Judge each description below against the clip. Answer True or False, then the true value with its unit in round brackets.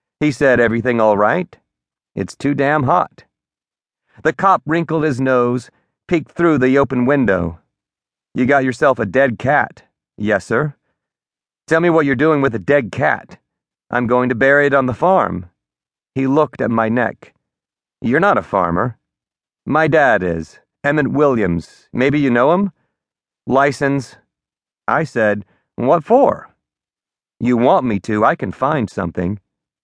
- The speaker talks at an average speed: True (150 wpm)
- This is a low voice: True (125 Hz)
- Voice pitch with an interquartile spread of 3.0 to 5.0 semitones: False (5.6 semitones)